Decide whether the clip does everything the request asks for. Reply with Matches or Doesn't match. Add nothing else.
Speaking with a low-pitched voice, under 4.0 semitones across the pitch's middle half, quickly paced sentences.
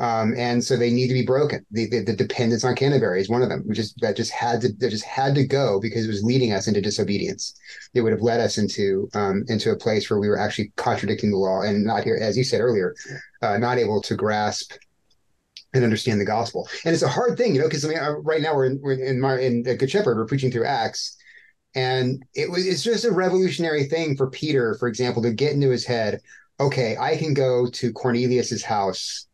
Matches